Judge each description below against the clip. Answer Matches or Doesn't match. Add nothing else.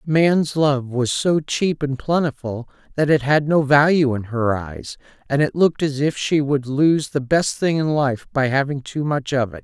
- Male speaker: Matches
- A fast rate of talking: Matches